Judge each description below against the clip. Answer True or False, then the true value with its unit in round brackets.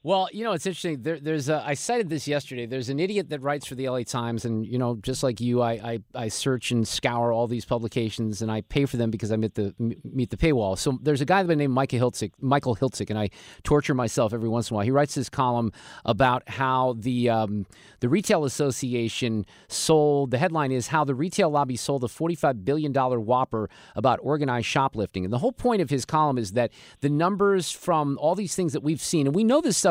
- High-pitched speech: False (130 Hz)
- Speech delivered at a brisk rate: True (240 wpm)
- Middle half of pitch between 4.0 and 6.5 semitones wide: True (4.5 semitones)